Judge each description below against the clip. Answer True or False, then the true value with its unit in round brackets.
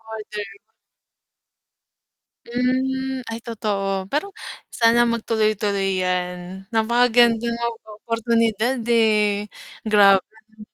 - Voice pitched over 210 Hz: True (220 Hz)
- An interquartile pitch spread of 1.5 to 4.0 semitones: True (2.5 semitones)